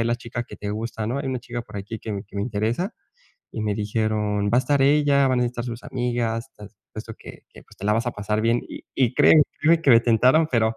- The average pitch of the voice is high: No, low, 115 Hz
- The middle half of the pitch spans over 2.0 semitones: Yes, average, 2.7 semitones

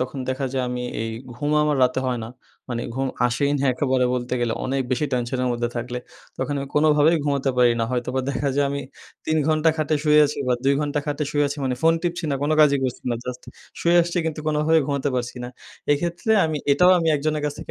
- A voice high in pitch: No, medium, 140 Hz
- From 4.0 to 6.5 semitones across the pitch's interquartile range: No, average, 3.1 semitones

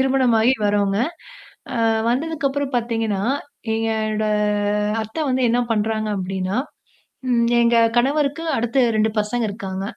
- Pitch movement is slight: No, average, 3.4 semitones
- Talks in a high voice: Yes, high, 225 Hz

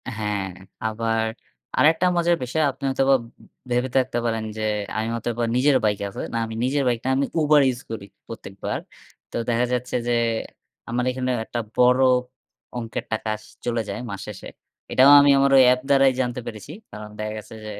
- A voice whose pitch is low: Yes, low, 120 Hz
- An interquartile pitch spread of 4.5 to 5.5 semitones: No, average, 3.2 semitones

